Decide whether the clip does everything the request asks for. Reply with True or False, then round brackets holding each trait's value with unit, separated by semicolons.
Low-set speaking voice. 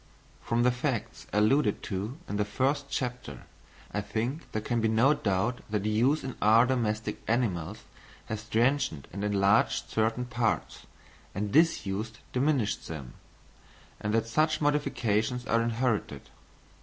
True (115 Hz)